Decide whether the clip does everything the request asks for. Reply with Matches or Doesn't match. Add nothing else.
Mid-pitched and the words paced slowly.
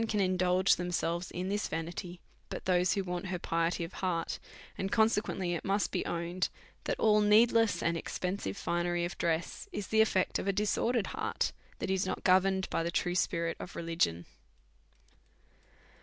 Doesn't match